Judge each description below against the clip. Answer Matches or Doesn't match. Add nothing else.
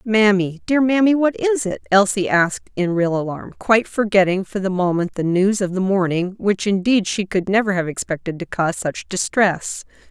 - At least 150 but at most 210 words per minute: Matches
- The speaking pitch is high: Matches